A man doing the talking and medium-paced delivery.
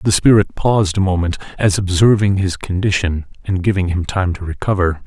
Yes: male; average, 180 wpm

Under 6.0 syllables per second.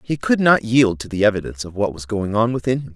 No: 6.3 syllables/s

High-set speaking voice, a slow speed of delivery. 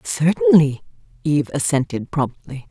No: medium, 145 Hz; slow, 90 wpm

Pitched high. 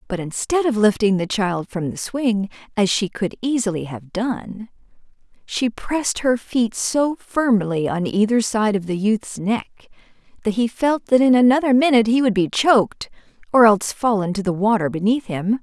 Yes: high, 220 Hz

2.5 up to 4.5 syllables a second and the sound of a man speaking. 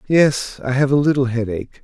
No: 5.4 syllables/s; male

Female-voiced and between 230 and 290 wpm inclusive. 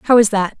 No: female; fast, 300 wpm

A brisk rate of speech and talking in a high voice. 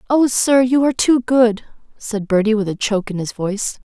Yes: fast, 215 wpm; high, 225 Hz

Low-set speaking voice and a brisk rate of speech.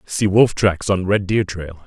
Yes: very low, 95 Hz; fast, 225 wpm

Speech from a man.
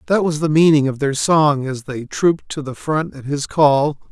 Yes: male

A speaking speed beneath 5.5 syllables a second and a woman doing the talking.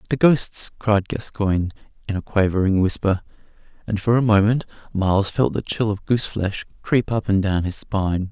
No: 5.2 syllables/s; male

